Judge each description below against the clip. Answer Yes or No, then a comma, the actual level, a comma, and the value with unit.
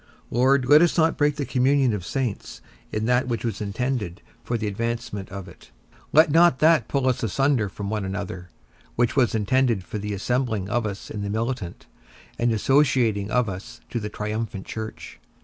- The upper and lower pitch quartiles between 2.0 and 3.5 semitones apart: No, average, 4.2 semitones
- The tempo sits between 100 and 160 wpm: No, average, 185 wpm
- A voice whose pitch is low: Yes, low, 115 Hz